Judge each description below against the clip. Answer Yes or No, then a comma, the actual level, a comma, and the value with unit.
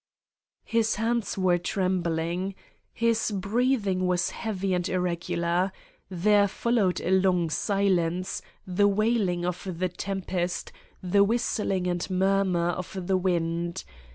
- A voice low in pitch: No, medium, 185 Hz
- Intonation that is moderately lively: No, narrow, 2.3 semitones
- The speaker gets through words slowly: Yes, slow, 125 wpm